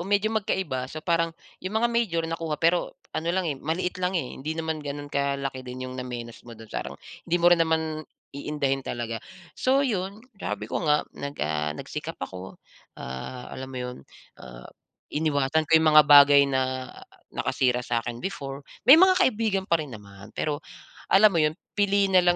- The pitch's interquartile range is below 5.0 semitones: No, wide, 5.5 semitones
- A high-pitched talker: No, medium, 150 Hz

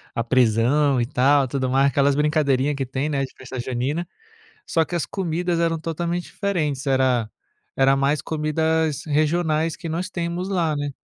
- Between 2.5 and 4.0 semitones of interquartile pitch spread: Yes, average, 3.6 semitones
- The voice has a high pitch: No, medium, 150 Hz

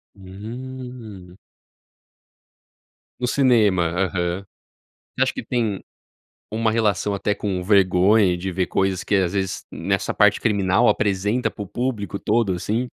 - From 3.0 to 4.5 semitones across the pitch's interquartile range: Yes, average, 3.3 semitones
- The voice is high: No, low, 100 Hz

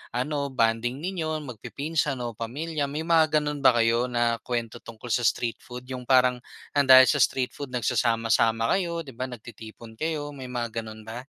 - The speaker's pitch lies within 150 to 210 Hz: No, low, 125 Hz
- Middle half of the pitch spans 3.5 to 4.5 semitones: Yes, average, 3.9 semitones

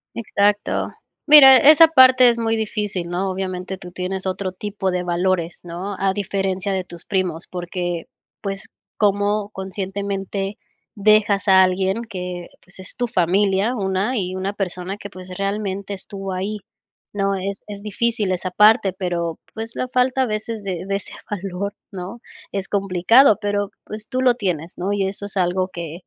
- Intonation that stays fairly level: Yes, narrow, 2.1 semitones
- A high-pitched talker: Yes, high, 195 Hz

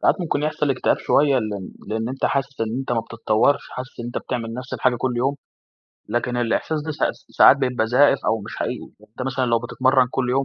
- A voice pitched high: No, low, 125 Hz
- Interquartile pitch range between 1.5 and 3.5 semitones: Yes, average, 2.7 semitones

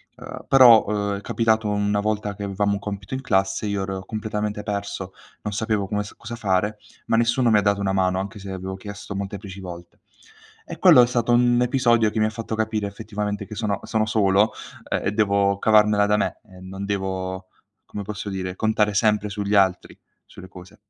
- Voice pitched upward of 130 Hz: No, low, 105 Hz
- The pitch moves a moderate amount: No, narrow, 1.9 semitones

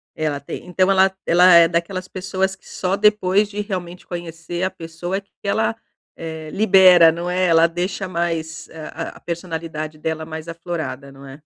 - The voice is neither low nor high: Yes, medium, 170 Hz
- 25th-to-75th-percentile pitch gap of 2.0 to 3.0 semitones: Yes, narrow, 2.6 semitones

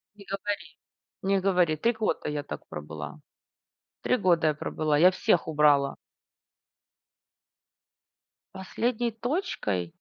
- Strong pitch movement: Yes, wide, 5.8 semitones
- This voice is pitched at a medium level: Yes, medium, 170 Hz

